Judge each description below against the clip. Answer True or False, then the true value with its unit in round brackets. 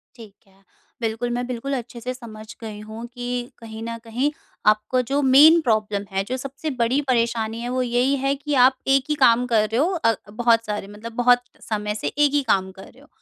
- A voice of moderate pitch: False (235 Hz)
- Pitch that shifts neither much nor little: True (3.0 semitones)